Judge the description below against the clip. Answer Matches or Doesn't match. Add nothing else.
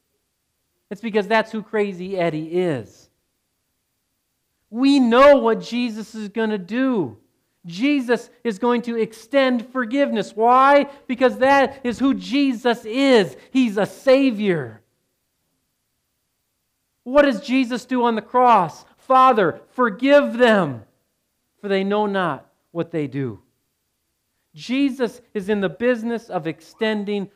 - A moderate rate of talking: Doesn't match